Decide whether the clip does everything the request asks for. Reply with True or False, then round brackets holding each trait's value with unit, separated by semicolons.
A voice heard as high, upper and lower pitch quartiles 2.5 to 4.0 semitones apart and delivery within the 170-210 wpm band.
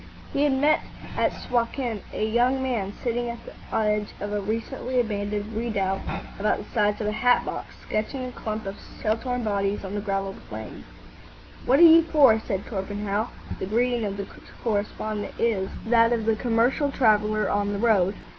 True (220 Hz; 2.9 semitones; 180 wpm)